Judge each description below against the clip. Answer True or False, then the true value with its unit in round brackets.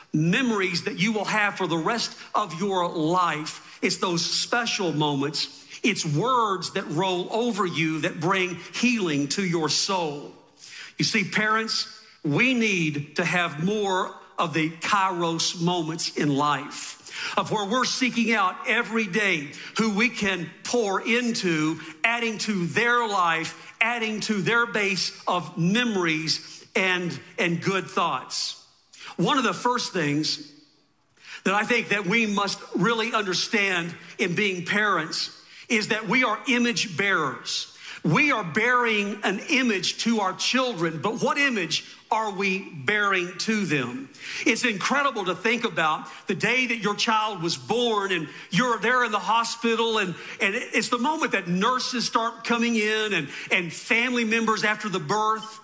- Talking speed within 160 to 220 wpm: False (150 wpm)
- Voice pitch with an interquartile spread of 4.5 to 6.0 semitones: True (4.9 semitones)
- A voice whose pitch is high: True (200 Hz)